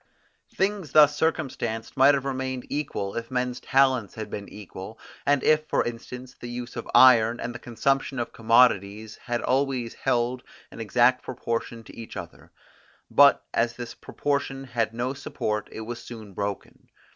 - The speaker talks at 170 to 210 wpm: No, average, 160 wpm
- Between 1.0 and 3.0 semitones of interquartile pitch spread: Yes, average, 2.7 semitones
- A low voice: Yes, low, 120 Hz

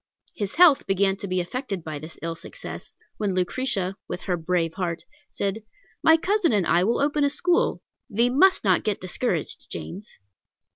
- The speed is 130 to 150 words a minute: No, average, 175 wpm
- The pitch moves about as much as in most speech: No, wide, 6.7 semitones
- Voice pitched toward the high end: Yes, high, 200 Hz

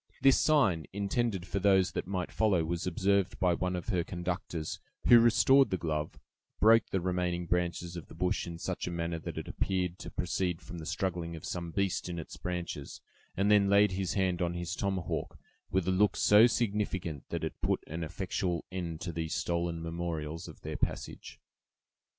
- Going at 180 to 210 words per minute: Yes, average, 190 wpm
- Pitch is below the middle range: Yes, very low, 90 Hz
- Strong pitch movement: No, narrow, 2.5 semitones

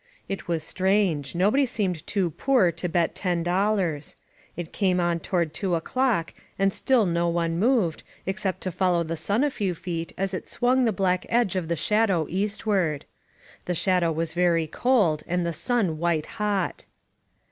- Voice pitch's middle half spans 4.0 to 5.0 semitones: No, average, 3.5 semitones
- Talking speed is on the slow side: No, average, 175 wpm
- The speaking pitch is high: No, medium, 180 Hz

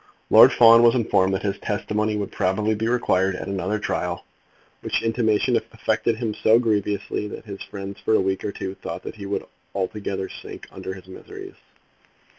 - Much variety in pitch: No, narrow, 2.4 semitones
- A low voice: Yes, low, 105 Hz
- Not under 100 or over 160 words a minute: No, average, 180 wpm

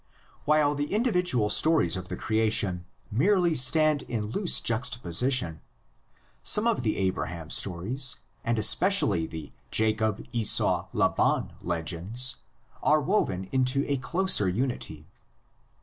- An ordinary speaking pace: No, slow, 115 wpm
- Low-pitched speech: Yes, low, 120 Hz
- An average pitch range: No, wide, 7.7 semitones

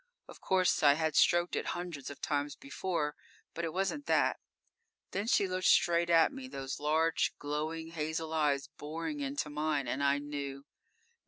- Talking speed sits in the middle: Yes, average, 165 wpm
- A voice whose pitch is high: No, medium, 160 Hz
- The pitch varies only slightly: No, average, 3.2 semitones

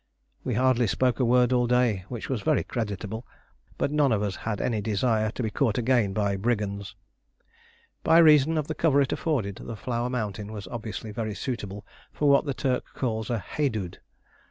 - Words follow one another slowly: No, average, 185 wpm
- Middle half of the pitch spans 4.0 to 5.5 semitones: No, average, 3.6 semitones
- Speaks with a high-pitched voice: No, low, 115 Hz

